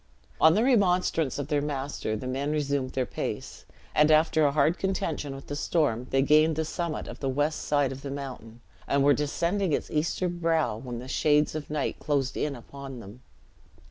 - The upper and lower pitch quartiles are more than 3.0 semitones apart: No, average, 2.7 semitones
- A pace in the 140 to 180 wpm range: No, average, 195 wpm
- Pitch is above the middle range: No, medium, 145 Hz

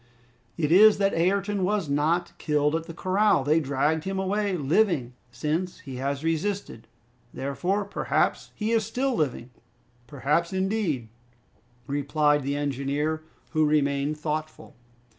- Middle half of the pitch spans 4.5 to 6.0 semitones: Yes, average, 5.1 semitones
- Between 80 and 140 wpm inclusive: Yes, slow, 135 wpm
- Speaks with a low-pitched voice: No, medium, 155 Hz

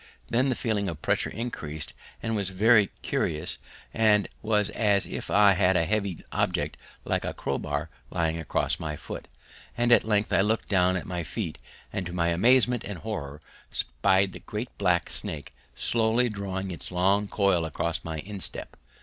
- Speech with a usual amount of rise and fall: Yes, average, 4.3 semitones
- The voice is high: No, very low, 95 Hz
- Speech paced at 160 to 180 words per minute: Yes, average, 170 wpm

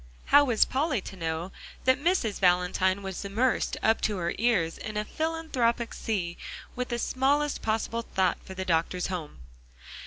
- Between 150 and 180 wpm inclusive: Yes, average, 160 wpm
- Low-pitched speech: No, high, 215 Hz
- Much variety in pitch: Yes, wide, 5.8 semitones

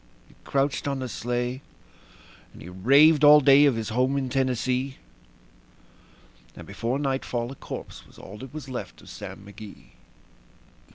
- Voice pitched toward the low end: Yes, low, 130 Hz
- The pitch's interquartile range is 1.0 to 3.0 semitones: Yes, narrow, 2.4 semitones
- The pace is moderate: Yes, average, 155 wpm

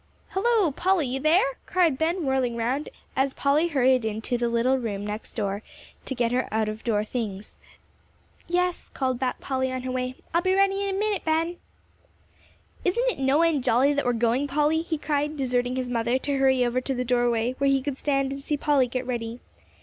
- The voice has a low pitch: No, very high, 265 Hz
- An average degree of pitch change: Yes, average, 4.1 semitones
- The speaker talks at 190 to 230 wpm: Yes, average, 200 wpm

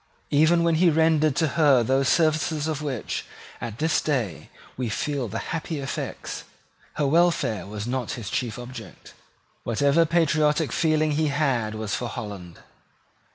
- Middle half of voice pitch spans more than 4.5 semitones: Yes, average, 4.9 semitones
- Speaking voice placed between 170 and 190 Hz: No, medium, 145 Hz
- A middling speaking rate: Yes, average, 150 wpm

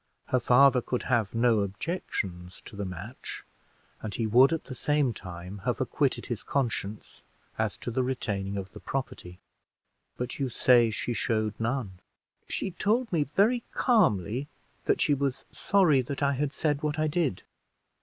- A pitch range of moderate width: No, wide, 5.9 semitones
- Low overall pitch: Yes, low, 125 Hz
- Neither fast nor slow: Yes, average, 165 wpm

